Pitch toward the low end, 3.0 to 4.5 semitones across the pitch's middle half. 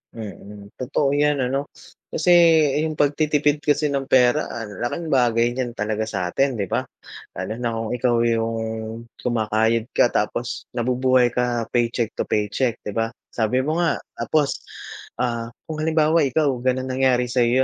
Yes: low, 125 Hz; average, 3.5 semitones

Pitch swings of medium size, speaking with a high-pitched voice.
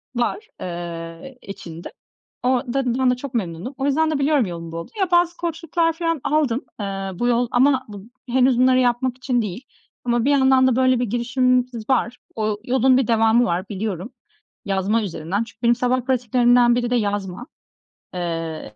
Yes: average, 4.3 semitones; high, 245 Hz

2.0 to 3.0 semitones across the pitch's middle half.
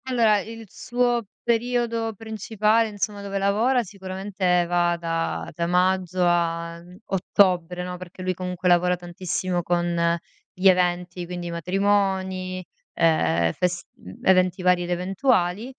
Yes: narrow, 2.6 semitones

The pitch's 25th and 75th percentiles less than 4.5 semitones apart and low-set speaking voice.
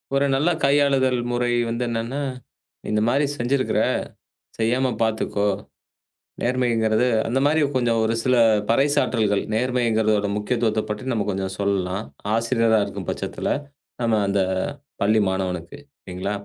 Yes: average, 3.5 semitones; low, 115 Hz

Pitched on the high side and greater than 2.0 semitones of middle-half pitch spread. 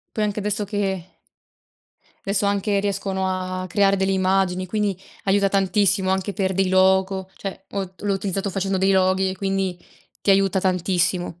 No: high, 195 Hz; narrow, 1.0 semitones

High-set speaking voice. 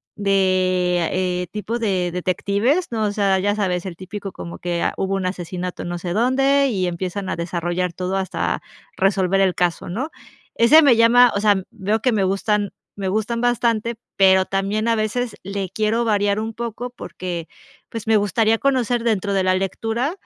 Yes: high, 200 Hz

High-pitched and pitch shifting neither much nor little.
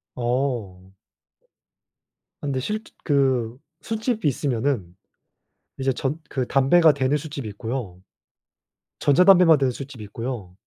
No: low, 135 Hz; average, 3.9 semitones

